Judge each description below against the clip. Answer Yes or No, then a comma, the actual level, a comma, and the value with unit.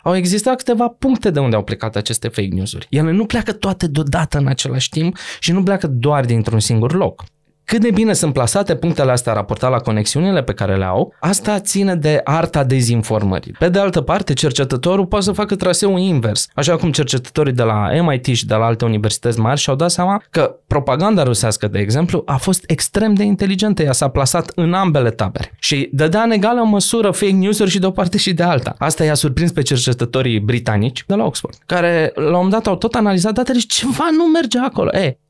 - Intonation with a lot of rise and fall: Yes, wide, 8.1 semitones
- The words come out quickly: Yes, fast, 210 wpm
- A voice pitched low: No, medium, 160 Hz